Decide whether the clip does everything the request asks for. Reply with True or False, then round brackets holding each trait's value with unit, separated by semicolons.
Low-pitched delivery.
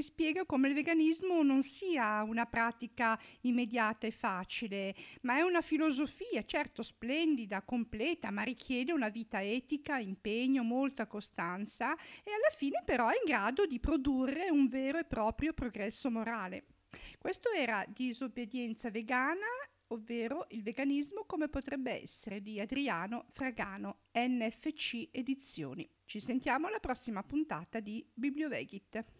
False (250 Hz)